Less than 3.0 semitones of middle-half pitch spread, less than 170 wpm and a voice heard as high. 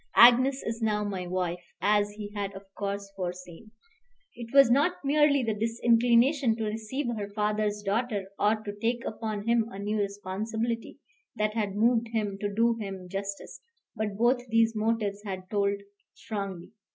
Yes: narrow, 2.4 semitones; average, 160 wpm; high, 215 Hz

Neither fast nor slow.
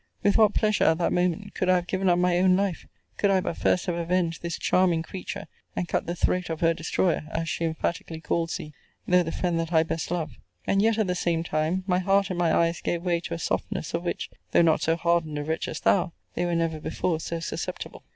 No: fast, 245 wpm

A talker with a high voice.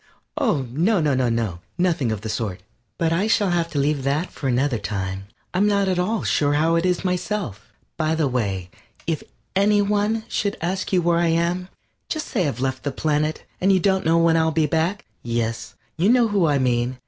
No: medium, 160 Hz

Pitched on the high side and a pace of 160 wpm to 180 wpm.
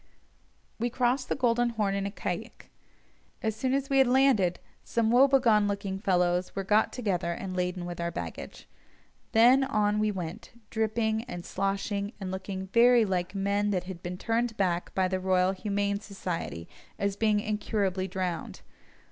Yes: high, 200 Hz; average, 165 wpm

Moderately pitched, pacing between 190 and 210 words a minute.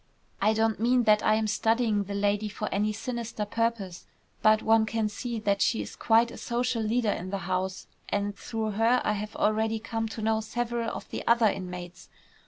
No: high, 220 Hz; average, 195 wpm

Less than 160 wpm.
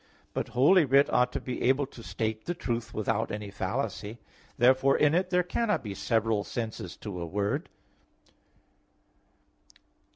Yes: average, 150 wpm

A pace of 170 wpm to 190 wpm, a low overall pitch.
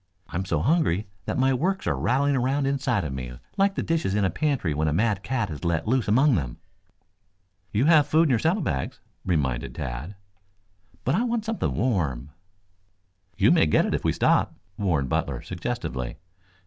Yes: average, 185 wpm; low, 110 Hz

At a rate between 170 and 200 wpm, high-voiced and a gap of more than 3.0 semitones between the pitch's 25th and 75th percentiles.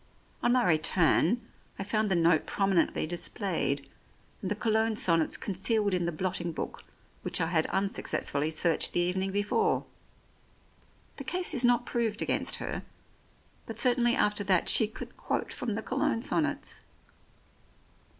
No: average, 145 wpm; high, 200 Hz; average, 4.7 semitones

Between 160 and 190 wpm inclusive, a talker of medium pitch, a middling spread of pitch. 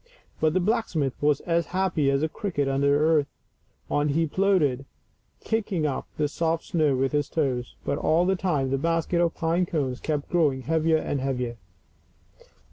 Yes: average, 175 wpm; medium, 155 Hz; average, 3.5 semitones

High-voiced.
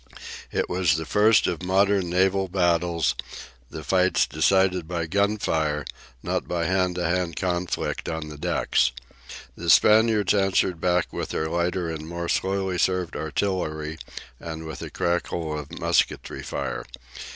No: very low, 90 Hz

